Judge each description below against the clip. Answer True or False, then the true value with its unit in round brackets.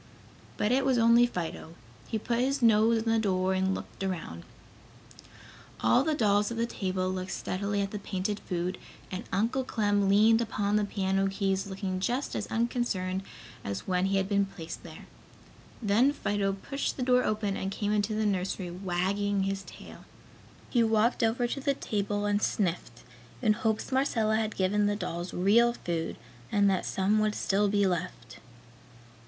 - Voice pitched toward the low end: False (205 Hz)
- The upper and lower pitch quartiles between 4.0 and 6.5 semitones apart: False (2.9 semitones)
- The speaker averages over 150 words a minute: True (170 wpm)